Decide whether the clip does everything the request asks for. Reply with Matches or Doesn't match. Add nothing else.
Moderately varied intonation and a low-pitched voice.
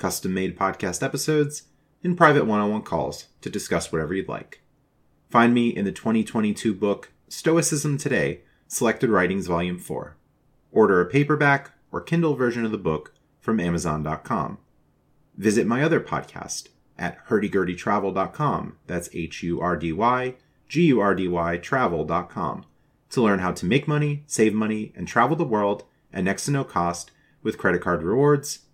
Doesn't match